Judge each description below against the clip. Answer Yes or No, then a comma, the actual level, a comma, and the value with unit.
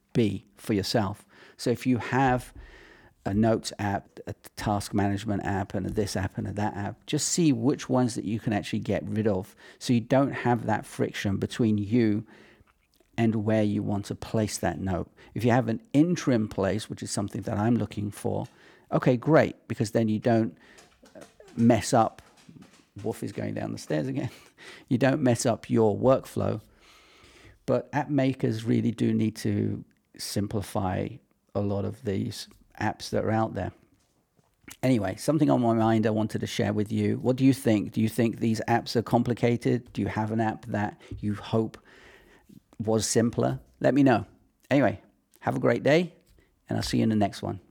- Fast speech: No, average, 185 wpm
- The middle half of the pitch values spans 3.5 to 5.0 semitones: No, narrow, 2.6 semitones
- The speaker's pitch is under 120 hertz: Yes, low, 110 Hz